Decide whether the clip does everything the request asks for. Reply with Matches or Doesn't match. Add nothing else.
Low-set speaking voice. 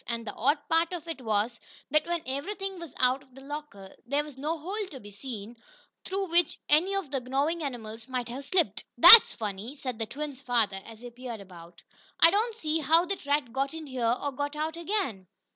Doesn't match